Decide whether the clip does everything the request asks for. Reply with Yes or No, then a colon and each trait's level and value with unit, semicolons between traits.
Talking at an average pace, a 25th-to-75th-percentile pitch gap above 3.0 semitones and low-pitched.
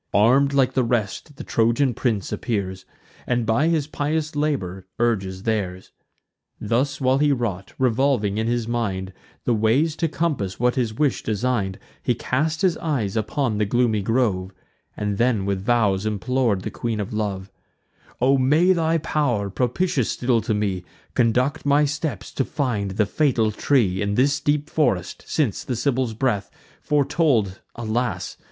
Yes: average, 155 wpm; average, 5.3 semitones; low, 120 Hz